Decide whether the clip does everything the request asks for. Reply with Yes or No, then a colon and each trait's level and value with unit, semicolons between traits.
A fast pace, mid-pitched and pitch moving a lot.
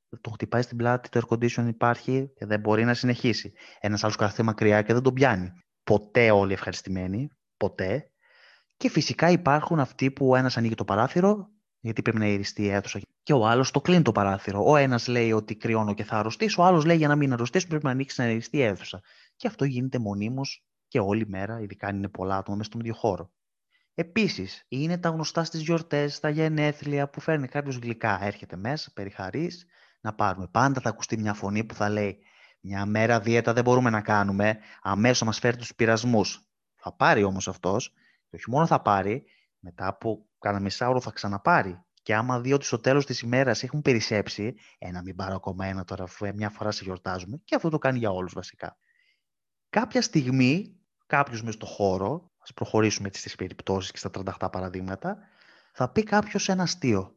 No: fast, 195 wpm; low, 115 Hz; wide, 5.7 semitones